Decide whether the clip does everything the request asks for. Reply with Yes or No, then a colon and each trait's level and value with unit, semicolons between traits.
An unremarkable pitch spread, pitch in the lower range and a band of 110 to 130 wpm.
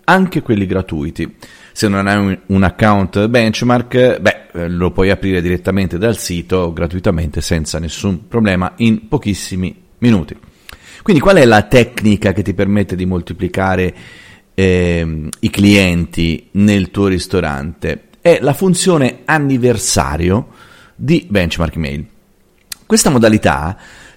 Yes: average, 4.6 semitones; low, 100 Hz; average, 120 wpm